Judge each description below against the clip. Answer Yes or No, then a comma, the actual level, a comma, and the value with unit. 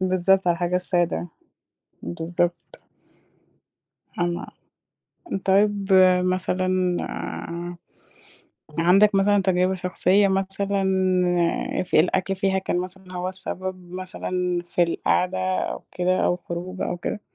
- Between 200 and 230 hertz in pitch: No, medium, 185 Hz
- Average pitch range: No, narrow, 1.3 semitones